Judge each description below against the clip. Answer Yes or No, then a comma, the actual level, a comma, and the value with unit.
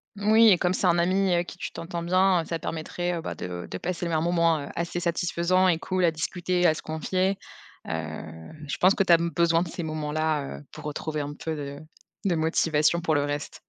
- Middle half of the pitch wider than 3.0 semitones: No, narrow, 2.4 semitones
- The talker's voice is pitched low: No, medium, 170 Hz